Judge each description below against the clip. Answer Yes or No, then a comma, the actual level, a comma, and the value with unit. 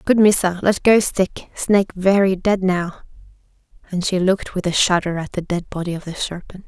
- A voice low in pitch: No, medium, 185 Hz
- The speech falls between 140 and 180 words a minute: No, average, 200 wpm